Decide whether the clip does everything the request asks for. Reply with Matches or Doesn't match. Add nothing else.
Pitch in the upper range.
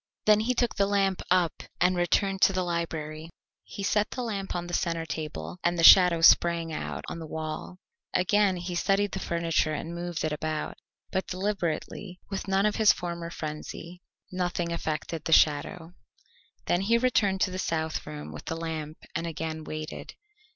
Doesn't match